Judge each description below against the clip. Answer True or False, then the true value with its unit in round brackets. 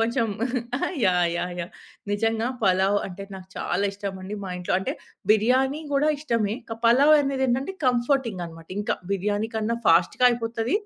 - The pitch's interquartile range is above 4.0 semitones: True (4.7 semitones)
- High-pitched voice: True (220 Hz)